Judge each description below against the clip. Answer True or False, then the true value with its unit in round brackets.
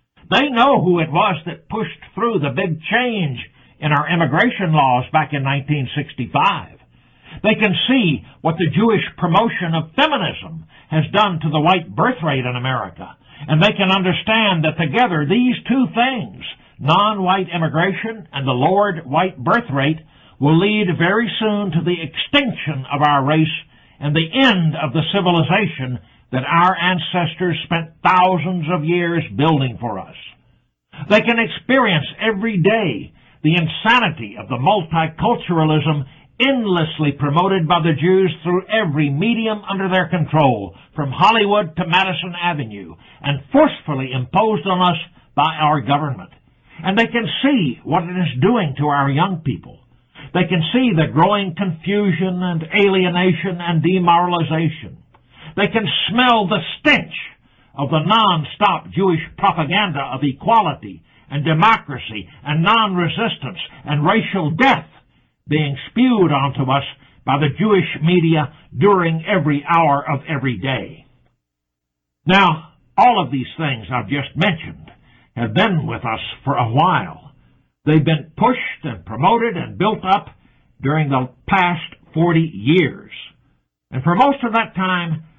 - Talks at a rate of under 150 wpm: True (140 wpm)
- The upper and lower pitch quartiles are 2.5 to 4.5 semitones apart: False (5.1 semitones)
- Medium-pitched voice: True (165 Hz)